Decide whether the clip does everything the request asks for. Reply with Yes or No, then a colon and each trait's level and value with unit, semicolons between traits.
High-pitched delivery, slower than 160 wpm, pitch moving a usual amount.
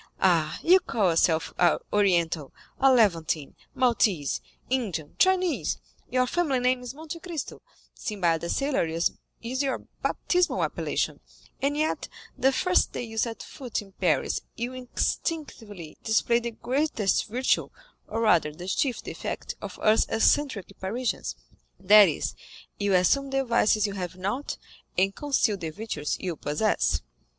No: high, 220 Hz; slow, 135 wpm; wide, 6.7 semitones